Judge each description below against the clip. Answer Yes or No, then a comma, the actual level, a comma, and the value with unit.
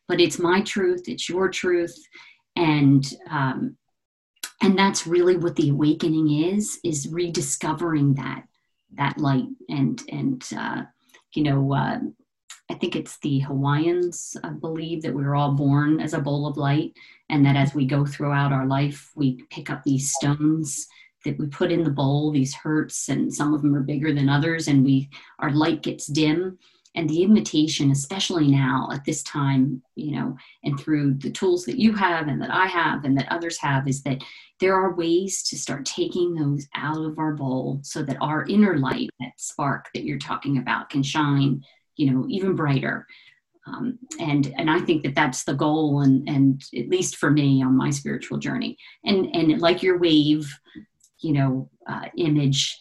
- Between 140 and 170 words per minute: No, average, 185 wpm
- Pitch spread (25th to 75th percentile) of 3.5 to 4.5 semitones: Yes, average, 3.8 semitones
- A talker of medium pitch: Yes, medium, 150 Hz